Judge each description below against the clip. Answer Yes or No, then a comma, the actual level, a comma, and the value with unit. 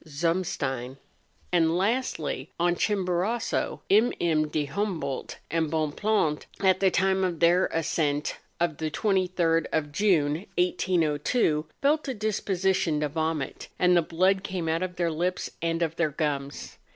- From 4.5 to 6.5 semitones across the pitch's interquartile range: No, average, 3.5 semitones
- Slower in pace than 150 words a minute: Yes, average, 140 wpm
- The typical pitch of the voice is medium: Yes, medium, 170 Hz